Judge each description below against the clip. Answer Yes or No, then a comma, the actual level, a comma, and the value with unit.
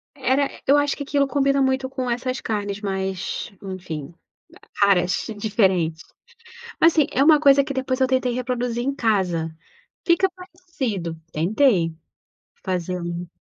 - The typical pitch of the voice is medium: No, high, 240 Hz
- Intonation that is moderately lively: No, wide, 6.7 semitones